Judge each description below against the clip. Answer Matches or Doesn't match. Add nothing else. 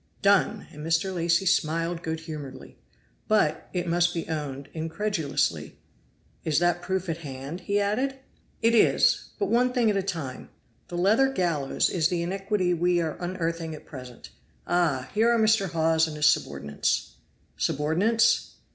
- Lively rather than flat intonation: Doesn't match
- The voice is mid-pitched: Matches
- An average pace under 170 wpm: Matches